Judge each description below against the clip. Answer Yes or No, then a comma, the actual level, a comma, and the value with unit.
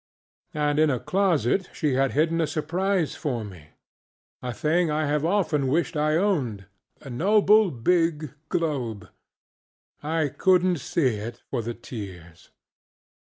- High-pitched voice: No, medium, 150 Hz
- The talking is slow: Yes, slow, 130 wpm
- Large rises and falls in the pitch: Yes, wide, 5.7 semitones